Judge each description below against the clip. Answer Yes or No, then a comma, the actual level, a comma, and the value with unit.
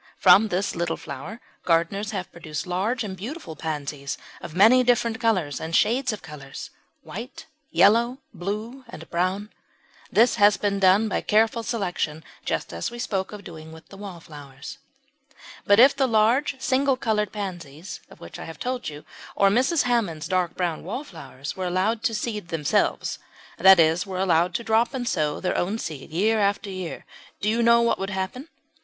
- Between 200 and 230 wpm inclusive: No, average, 175 wpm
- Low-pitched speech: No, high, 195 Hz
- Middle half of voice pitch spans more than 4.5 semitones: Yes, wide, 5.5 semitones